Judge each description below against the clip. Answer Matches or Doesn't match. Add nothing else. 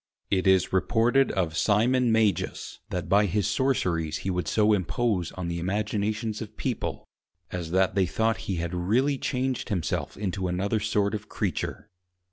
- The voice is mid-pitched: Doesn't match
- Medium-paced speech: Matches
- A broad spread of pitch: Doesn't match